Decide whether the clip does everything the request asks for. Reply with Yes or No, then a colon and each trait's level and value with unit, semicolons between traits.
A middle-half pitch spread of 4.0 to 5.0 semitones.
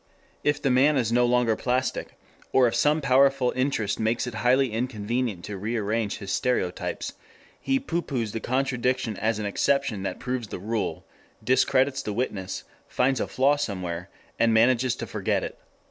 No: average, 3.4 semitones